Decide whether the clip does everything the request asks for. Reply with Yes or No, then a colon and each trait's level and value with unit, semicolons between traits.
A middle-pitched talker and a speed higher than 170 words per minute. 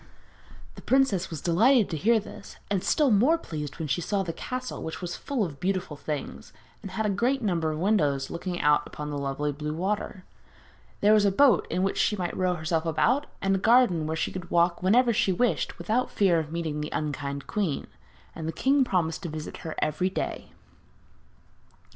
Yes: medium, 180 Hz; average, 200 wpm